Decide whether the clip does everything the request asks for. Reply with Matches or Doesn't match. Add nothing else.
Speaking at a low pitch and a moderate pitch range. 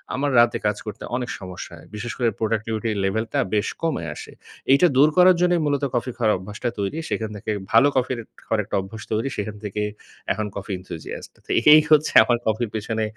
Matches